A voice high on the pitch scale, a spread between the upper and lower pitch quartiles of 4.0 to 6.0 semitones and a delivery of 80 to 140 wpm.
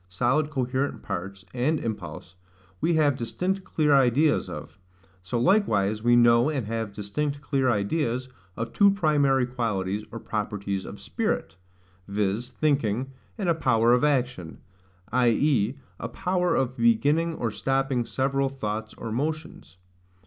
No: low, 125 Hz; average, 5.0 semitones; slow, 135 wpm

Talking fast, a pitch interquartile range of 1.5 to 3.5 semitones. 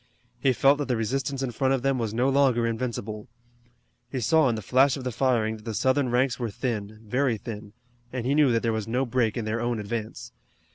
Yes: fast, 230 wpm; average, 3.0 semitones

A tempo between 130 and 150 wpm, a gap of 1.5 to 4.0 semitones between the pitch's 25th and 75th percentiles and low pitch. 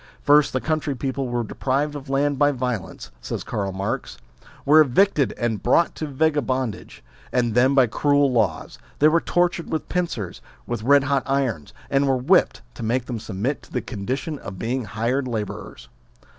No: average, 170 wpm; average, 3.6 semitones; low, 130 Hz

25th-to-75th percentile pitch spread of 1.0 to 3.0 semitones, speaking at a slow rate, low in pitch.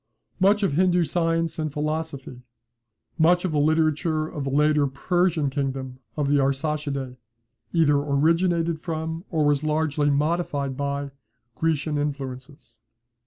No: narrow, 2.6 semitones; slow, 125 wpm; medium, 150 Hz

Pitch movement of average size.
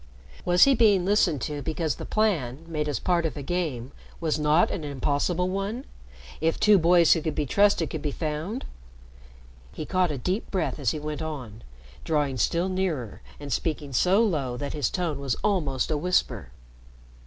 Yes: average, 4.0 semitones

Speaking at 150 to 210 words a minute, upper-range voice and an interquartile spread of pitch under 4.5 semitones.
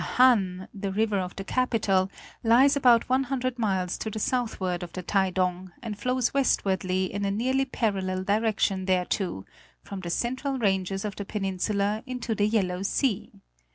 Yes: average, 165 wpm; high, 205 Hz; average, 4.1 semitones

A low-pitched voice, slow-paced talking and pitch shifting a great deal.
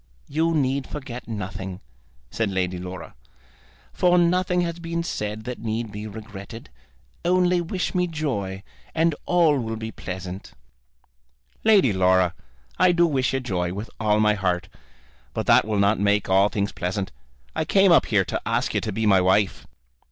No: low, 110 Hz; average, 165 wpm; wide, 8.9 semitones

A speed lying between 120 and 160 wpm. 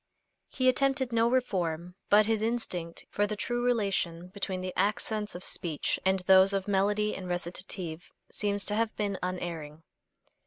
Yes: average, 155 wpm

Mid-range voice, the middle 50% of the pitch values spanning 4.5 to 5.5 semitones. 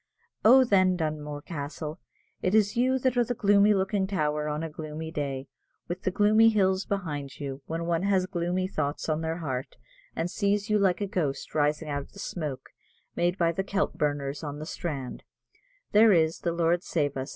Yes: medium, 170 Hz; average, 4.9 semitones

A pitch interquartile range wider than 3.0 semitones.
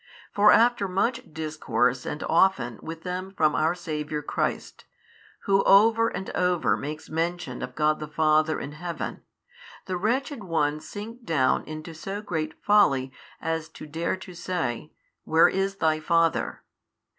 Yes: average, 4.0 semitones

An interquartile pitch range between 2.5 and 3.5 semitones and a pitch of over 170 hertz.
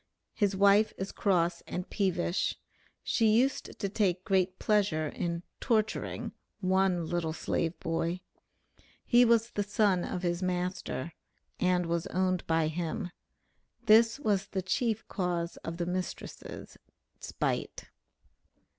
Yes: average, 3.1 semitones; medium, 185 Hz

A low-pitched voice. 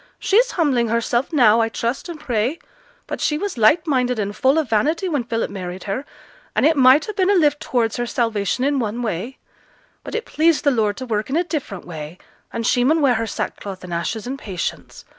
No: high, 245 Hz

